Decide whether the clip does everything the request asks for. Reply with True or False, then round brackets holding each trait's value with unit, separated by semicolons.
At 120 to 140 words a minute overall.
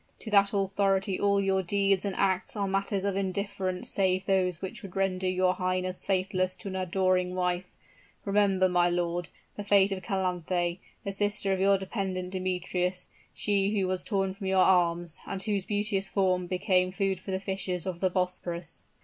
False (175 wpm)